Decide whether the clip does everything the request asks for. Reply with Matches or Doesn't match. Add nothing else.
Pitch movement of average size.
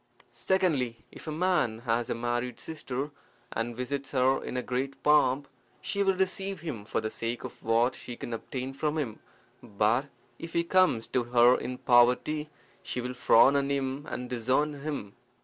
Matches